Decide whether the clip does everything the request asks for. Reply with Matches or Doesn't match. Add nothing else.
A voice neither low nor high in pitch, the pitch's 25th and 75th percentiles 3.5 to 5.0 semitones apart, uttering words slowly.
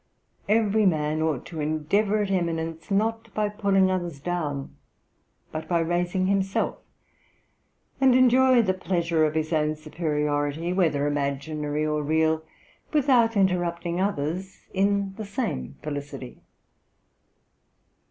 Matches